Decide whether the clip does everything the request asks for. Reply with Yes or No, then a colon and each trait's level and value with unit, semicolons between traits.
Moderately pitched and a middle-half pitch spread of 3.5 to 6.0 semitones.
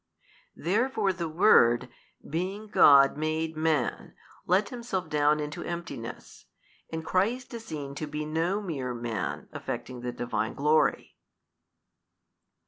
Yes: medium, 155 Hz; average, 5.0 semitones